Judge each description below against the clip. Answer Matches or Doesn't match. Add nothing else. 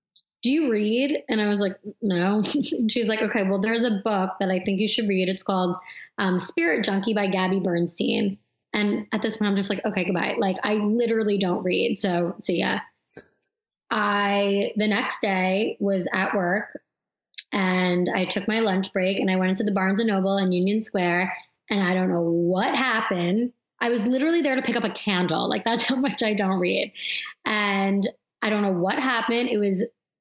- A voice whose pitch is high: Matches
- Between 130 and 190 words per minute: Doesn't match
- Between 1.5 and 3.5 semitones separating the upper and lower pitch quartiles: Matches